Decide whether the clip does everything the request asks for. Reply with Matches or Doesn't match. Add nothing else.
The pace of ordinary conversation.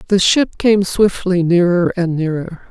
Matches